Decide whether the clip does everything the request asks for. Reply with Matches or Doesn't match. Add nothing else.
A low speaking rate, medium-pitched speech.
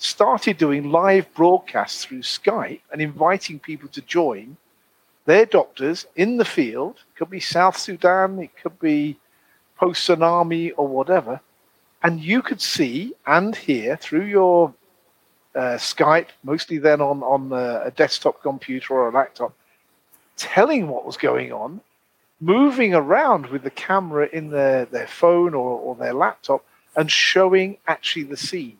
Doesn't match